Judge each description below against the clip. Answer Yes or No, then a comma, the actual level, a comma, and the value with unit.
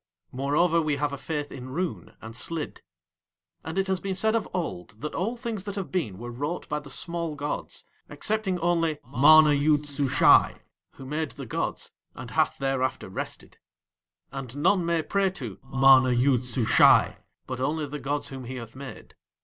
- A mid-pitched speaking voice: Yes, medium, 145 Hz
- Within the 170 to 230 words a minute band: Yes, average, 175 wpm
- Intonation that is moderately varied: Yes, average, 4.5 semitones